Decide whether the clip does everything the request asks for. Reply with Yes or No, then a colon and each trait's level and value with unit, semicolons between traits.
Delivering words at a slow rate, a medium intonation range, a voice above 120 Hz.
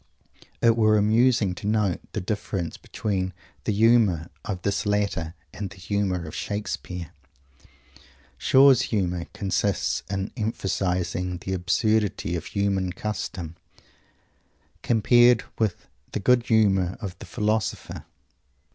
No: slow, 115 wpm; average, 3.0 semitones; low, 100 Hz